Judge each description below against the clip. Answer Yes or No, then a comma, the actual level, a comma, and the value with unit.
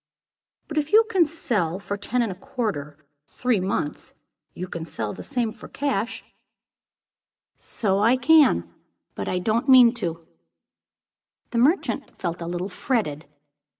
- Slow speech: No, average, 155 wpm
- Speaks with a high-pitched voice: Yes, high, 215 Hz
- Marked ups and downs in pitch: Yes, wide, 6.9 semitones